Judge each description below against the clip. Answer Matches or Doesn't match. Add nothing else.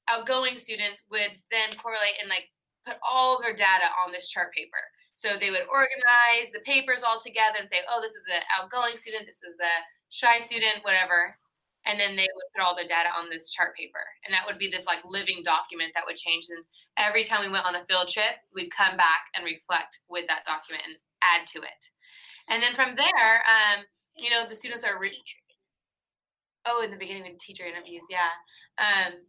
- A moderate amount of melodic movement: Matches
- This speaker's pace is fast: Matches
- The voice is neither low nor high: Doesn't match